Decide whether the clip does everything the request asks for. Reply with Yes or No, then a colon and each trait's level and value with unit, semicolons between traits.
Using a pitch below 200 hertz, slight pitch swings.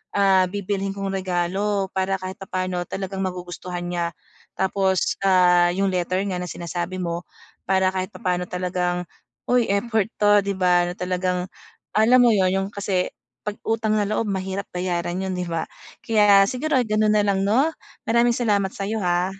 Yes: high, 190 Hz; narrow, 2.1 semitones